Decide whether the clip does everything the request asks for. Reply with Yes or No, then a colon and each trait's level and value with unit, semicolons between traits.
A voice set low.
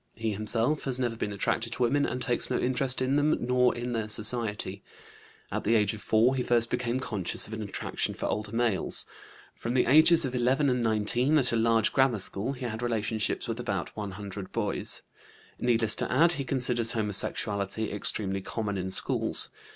Yes: low, 115 Hz